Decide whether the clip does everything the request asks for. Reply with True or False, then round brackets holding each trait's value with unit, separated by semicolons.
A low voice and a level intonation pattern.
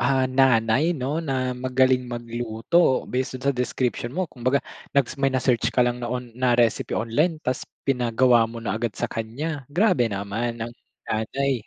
True (125 Hz; 2.3 semitones)